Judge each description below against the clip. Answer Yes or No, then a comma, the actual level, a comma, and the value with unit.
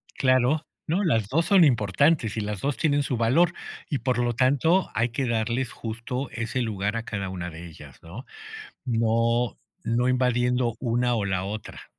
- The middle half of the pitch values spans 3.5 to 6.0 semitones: No, average, 3.0 semitones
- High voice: No, low, 120 Hz